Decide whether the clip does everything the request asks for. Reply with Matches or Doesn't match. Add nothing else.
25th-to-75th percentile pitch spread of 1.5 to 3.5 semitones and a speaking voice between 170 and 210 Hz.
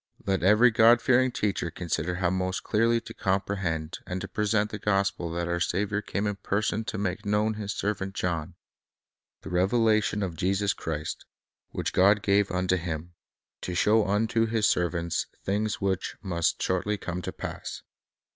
Doesn't match